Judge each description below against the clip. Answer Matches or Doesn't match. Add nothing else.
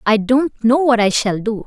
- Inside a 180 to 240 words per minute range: Doesn't match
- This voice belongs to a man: Doesn't match